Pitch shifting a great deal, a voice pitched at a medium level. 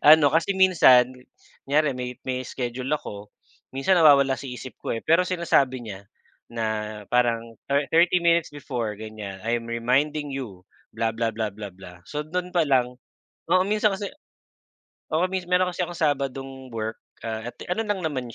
No: wide, 6.3 semitones; low, 130 Hz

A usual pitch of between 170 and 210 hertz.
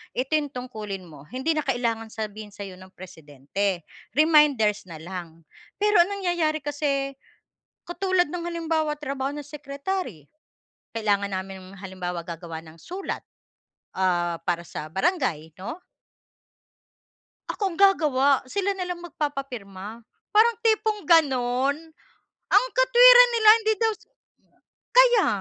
No: very high, 270 Hz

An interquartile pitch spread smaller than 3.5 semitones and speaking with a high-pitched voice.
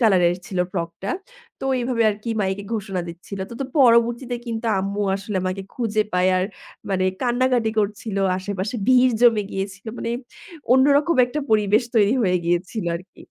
No: average, 3.9 semitones; high, 210 Hz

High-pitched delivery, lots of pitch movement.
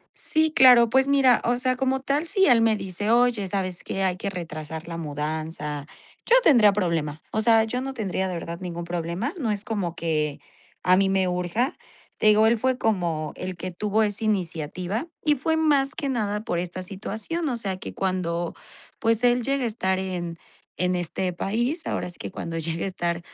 Yes: high, 195 Hz; wide, 5.9 semitones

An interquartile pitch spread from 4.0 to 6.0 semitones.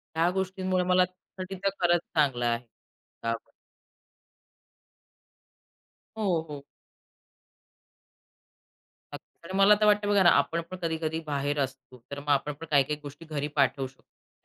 Yes: average, 4.7 semitones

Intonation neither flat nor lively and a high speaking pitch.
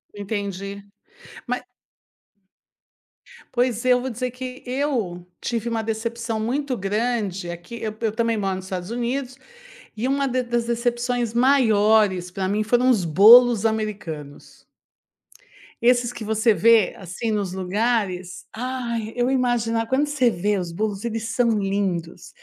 Yes: average, 3.5 semitones; high, 225 Hz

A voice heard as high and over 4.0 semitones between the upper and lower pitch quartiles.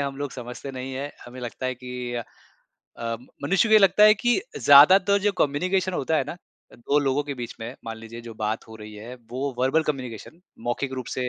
No: low, 135 Hz; average, 4.8 semitones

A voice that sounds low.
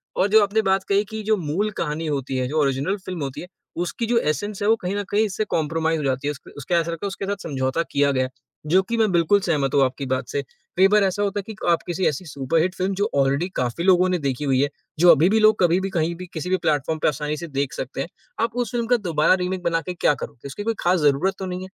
No: medium, 170 Hz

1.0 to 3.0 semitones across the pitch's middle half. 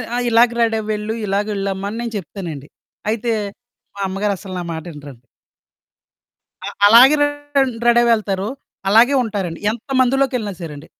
No: average, 3.5 semitones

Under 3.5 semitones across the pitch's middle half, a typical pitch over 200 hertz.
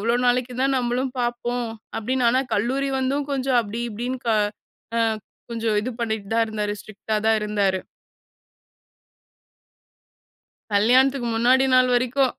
Yes: average, 2.9 semitones; high, 240 Hz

